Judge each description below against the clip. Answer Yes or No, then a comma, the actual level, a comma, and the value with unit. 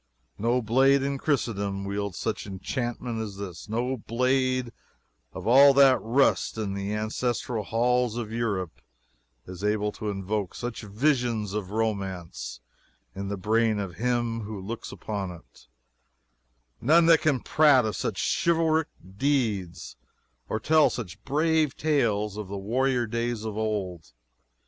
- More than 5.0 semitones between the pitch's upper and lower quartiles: No, average, 4.1 semitones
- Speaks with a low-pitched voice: Yes, low, 110 Hz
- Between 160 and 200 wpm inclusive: No, average, 140 wpm